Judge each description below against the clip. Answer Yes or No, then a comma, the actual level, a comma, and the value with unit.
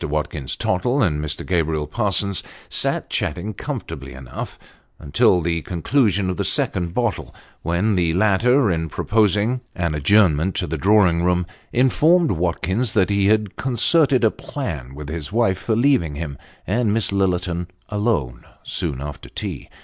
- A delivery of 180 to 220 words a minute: No, average, 150 wpm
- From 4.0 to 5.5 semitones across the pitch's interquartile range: Yes, average, 5.1 semitones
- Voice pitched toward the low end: Yes, very low, 95 Hz